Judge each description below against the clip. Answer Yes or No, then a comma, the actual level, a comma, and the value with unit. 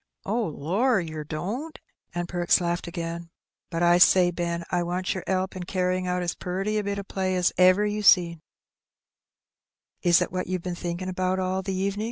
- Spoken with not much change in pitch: Yes, narrow, 1.7 semitones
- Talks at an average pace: Yes, average, 195 wpm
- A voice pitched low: No, medium, 185 Hz